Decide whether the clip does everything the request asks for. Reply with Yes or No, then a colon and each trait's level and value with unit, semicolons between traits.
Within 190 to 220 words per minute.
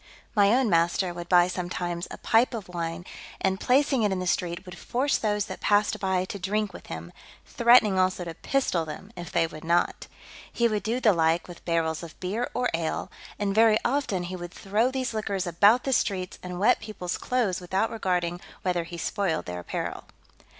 Yes: average, 200 wpm